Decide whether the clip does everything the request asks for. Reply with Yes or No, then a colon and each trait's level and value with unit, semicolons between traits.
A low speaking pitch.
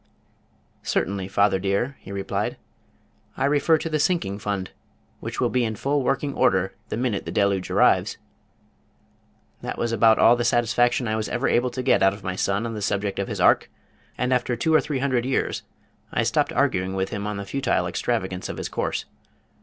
Yes: low, 110 Hz